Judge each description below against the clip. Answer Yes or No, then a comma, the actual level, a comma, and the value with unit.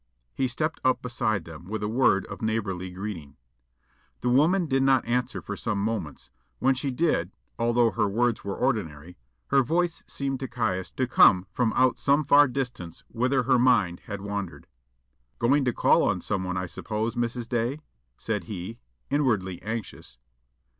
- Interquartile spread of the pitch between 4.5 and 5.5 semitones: Yes, average, 4.8 semitones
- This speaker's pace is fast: No, average, 165 wpm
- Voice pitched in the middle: No, low, 115 Hz